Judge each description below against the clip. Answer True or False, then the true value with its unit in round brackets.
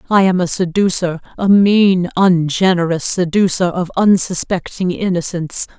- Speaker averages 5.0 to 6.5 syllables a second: False (4.6 syllables/s)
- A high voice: False (180 Hz)